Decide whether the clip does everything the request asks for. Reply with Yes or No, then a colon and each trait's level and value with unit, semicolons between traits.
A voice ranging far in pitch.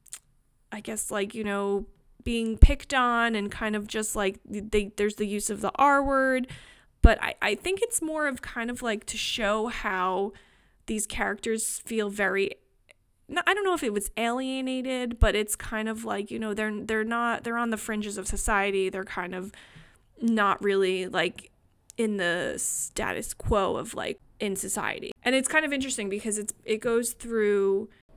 No: average, 2.8 semitones